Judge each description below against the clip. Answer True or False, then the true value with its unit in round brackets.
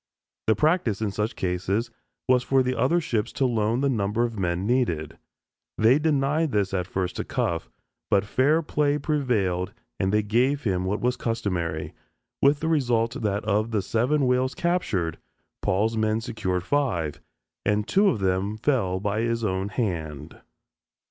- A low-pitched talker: True (110 Hz)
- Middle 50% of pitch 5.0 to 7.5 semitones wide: True (5.3 semitones)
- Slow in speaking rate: False (160 wpm)